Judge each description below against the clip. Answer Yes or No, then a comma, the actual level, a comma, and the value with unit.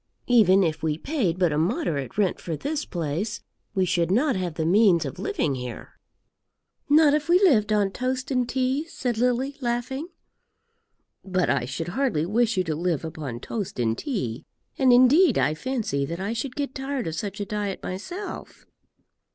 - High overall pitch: Yes, high, 205 Hz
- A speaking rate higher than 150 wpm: Yes, average, 175 wpm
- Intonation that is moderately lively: No, wide, 7.9 semitones